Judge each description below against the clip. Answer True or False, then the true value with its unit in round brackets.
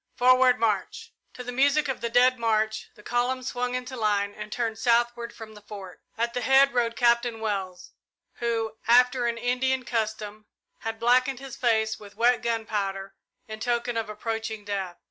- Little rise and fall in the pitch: True (2.3 semitones)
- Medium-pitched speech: False (235 Hz)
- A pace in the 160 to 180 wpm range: True (170 wpm)